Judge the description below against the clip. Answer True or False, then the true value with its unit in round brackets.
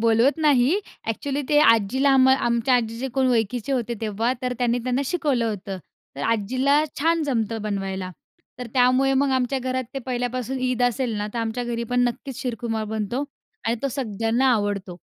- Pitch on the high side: True (245 Hz)